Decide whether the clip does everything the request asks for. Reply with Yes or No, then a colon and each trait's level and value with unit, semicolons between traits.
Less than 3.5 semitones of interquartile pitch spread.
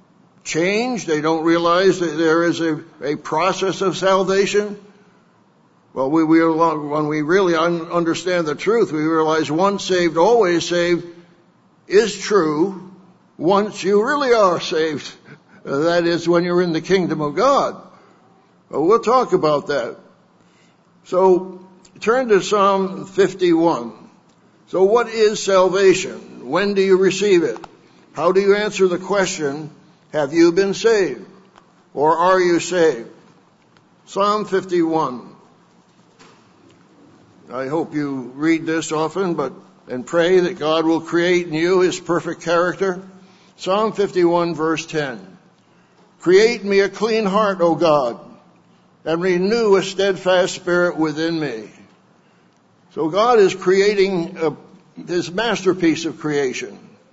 Yes: average, 3.0 semitones